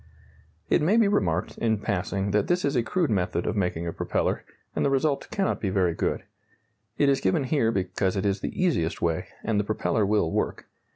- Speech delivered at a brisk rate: Yes, fast, 210 wpm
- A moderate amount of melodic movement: No, wide, 6.8 semitones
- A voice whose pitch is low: Yes, low, 105 Hz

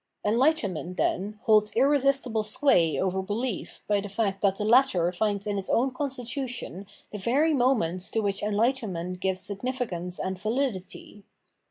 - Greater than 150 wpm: No, average, 145 wpm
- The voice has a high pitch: Yes, high, 210 Hz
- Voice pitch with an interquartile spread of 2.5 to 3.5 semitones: No, average, 5.0 semitones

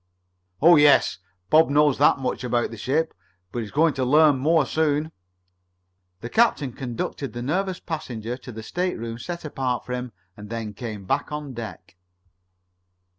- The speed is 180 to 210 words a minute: No, average, 160 wpm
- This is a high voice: No, low, 135 Hz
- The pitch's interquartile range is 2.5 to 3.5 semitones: No, average, 4.7 semitones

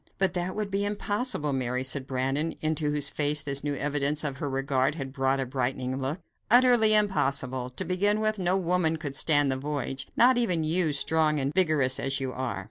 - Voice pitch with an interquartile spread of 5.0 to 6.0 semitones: Yes, average, 5.3 semitones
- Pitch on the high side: No, medium, 150 Hz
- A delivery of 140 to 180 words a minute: No, average, 200 wpm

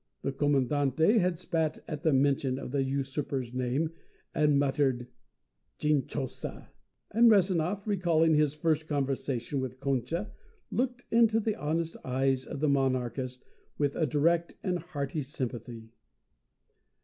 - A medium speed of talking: No, slow, 125 wpm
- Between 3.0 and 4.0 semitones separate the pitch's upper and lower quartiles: Yes, average, 3.7 semitones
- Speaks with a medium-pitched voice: Yes, medium, 145 Hz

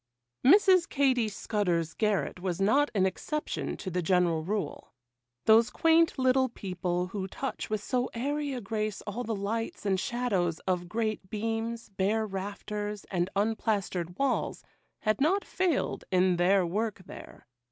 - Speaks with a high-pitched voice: Yes, high, 210 Hz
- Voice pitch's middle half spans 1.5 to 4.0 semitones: No, average, 4.6 semitones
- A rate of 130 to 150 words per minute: Yes, average, 145 wpm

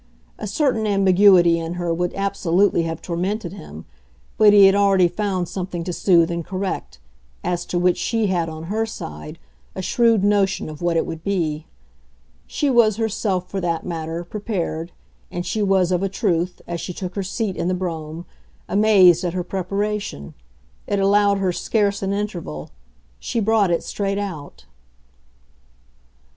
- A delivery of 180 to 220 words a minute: No, average, 165 wpm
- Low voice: No, medium, 185 Hz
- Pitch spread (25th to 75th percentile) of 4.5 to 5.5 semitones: No, average, 3.0 semitones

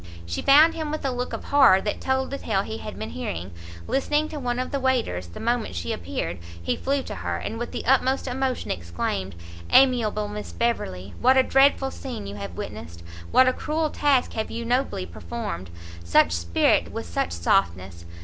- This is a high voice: Yes, high, 230 Hz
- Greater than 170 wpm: Yes, average, 195 wpm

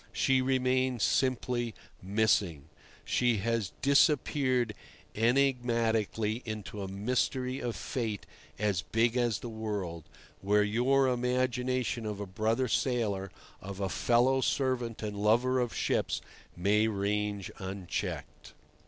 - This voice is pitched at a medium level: No, low, 115 Hz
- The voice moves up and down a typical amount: Yes, average, 3.6 semitones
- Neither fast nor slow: No, slow, 115 wpm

